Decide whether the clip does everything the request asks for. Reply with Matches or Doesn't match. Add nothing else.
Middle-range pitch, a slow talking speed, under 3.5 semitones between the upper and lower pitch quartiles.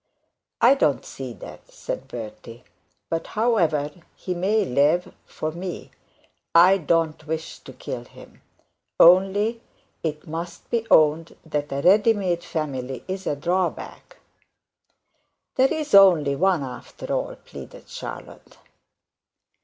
Doesn't match